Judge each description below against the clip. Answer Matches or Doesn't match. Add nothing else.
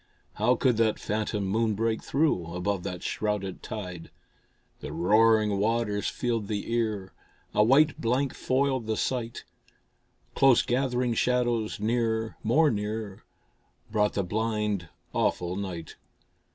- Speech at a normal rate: Doesn't match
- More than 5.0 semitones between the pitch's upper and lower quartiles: Doesn't match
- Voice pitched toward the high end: Doesn't match